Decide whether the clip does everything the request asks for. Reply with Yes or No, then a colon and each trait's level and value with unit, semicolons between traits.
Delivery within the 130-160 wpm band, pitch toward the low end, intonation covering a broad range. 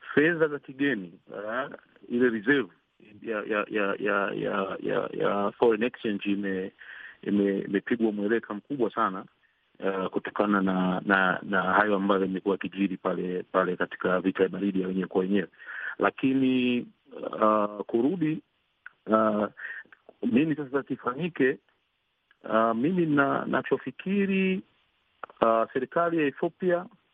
No: average, 120 wpm; low, 105 Hz; wide, 6.3 semitones